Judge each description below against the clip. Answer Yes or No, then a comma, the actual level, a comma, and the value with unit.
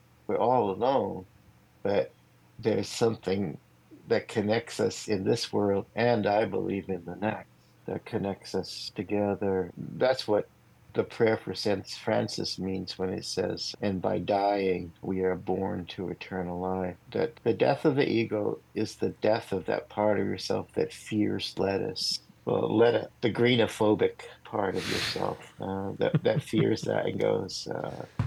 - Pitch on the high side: No, low, 100 Hz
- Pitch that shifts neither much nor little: No, narrow, 2.2 semitones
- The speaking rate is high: No, average, 155 wpm